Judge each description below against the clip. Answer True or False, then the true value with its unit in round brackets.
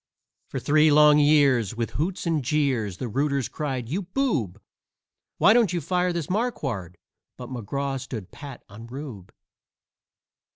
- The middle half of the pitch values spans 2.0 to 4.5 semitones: False (4.9 semitones)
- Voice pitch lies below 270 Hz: True (140 Hz)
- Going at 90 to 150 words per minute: True (140 wpm)